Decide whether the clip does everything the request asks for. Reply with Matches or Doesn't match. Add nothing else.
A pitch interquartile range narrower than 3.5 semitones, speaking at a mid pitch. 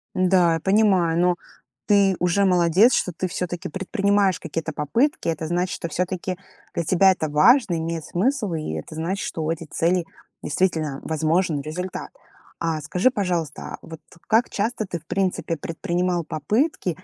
Matches